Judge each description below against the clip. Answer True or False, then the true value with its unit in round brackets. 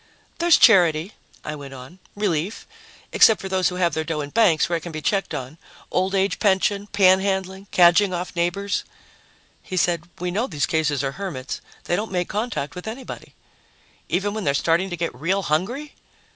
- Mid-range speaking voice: True (180 Hz)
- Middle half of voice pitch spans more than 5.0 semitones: False (3.8 semitones)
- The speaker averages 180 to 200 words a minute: True (185 wpm)